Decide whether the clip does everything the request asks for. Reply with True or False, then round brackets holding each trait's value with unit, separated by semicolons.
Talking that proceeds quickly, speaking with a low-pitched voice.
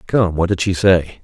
True (245 wpm; 90 Hz)